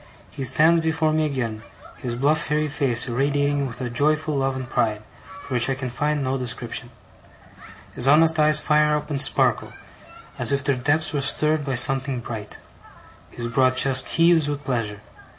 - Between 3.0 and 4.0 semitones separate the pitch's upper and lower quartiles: Yes, average, 3.3 semitones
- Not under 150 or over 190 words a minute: Yes, average, 175 wpm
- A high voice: No, medium, 140 Hz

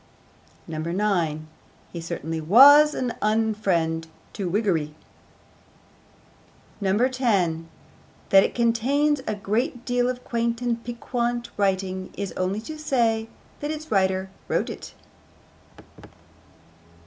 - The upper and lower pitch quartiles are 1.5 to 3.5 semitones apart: No, average, 4.7 semitones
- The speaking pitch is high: Yes, high, 215 Hz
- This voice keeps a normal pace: No, slow, 100 wpm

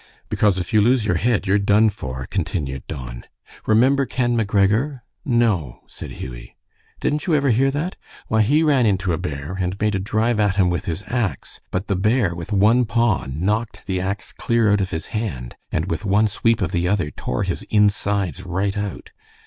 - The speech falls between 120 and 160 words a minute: No, average, 195 wpm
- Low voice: Yes, low, 100 Hz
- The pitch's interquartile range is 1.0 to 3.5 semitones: No, average, 4.2 semitones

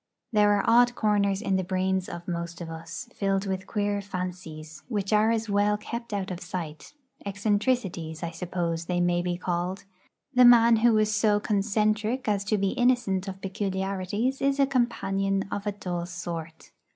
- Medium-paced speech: Yes, average, 175 wpm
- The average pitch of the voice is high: Yes, high, 195 Hz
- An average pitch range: Yes, average, 3.0 semitones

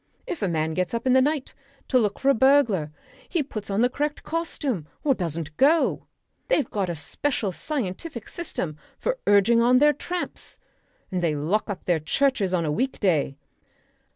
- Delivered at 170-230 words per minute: Yes, average, 180 wpm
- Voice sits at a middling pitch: No, high, 225 Hz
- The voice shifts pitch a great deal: Yes, wide, 7.9 semitones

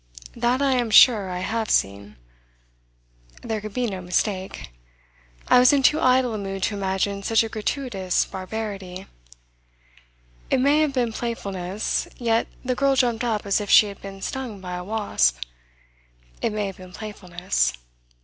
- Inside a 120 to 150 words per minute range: No, average, 160 wpm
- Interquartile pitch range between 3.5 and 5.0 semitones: Yes, average, 4.1 semitones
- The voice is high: Yes, high, 210 Hz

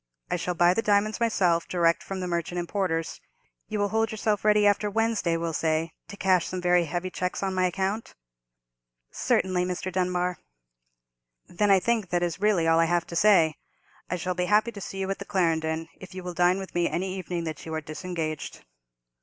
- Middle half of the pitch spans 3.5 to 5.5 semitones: No, average, 2.7 semitones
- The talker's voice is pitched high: No, medium, 180 Hz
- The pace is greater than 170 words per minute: Yes, fast, 205 wpm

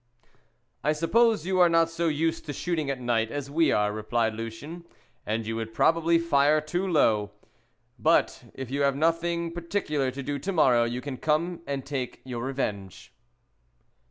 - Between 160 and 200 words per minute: Yes, average, 170 wpm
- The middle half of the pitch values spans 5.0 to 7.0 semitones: Yes, wide, 5.5 semitones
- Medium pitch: Yes, medium, 145 Hz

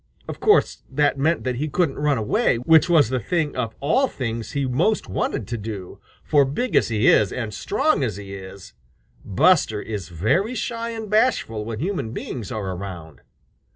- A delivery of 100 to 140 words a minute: No, average, 185 wpm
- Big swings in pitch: Yes, wide, 7.9 semitones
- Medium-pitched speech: No, low, 125 Hz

